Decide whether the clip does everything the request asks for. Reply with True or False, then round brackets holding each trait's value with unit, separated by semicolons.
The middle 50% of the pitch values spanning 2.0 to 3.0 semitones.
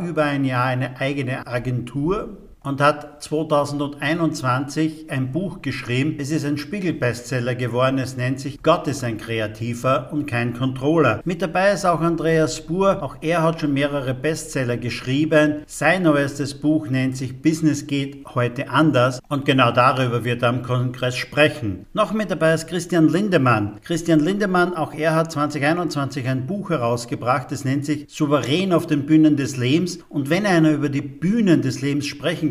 False (3.4 semitones)